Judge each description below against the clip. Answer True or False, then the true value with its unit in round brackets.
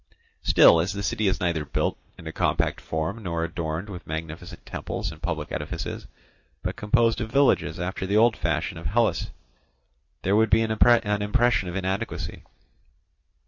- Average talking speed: True (160 wpm)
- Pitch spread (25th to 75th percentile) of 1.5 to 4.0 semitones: False (4.5 semitones)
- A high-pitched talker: False (100 Hz)